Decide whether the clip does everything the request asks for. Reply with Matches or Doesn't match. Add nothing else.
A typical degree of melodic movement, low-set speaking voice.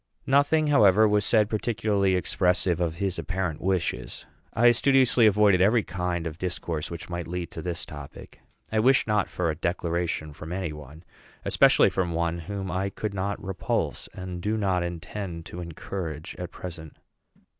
Matches